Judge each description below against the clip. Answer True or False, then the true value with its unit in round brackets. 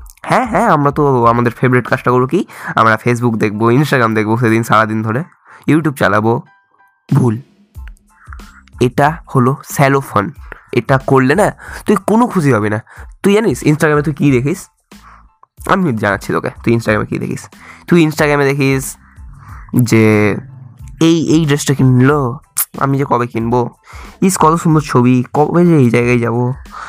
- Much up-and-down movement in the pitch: False (4.8 semitones)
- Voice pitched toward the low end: True (130 Hz)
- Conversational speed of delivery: False (145 wpm)